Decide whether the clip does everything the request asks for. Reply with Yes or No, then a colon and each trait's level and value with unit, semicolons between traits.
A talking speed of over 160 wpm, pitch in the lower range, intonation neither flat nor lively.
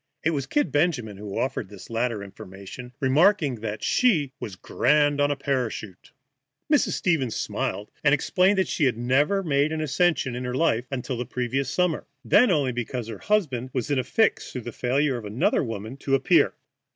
Yes: average, 190 wpm; low, 130 Hz; average, 4.3 semitones